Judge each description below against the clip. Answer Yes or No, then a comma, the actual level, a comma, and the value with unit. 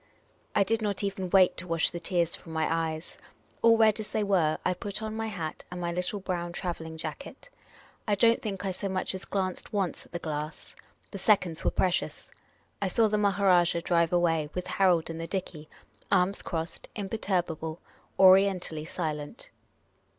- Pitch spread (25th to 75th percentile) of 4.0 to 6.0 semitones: No, average, 3.2 semitones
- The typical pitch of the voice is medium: Yes, medium, 180 Hz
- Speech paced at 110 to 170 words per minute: No, average, 180 wpm